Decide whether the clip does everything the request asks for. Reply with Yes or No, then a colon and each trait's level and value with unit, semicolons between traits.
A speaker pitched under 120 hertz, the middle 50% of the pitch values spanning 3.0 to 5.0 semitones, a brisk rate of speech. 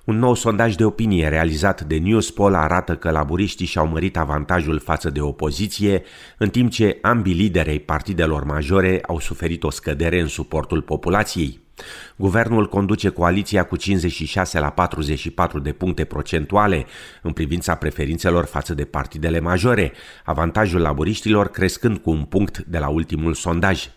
No: very low, 85 Hz; average, 4.0 semitones; average, 150 wpm